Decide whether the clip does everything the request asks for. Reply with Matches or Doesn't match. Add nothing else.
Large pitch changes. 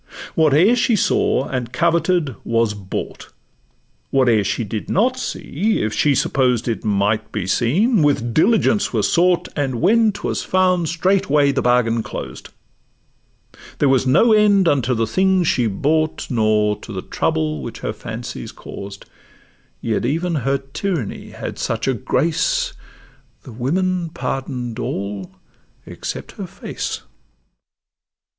Matches